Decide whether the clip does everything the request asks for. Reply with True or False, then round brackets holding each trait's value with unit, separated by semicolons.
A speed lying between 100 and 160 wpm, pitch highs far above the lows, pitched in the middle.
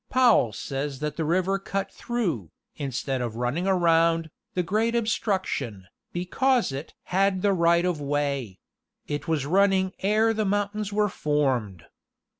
True (145 wpm; 6.0 semitones; 170 Hz)